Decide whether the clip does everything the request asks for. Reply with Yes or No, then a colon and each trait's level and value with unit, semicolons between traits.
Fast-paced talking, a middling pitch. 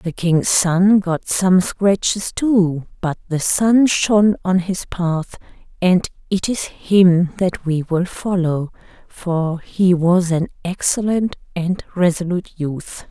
No: slow, 135 wpm; medium, 180 Hz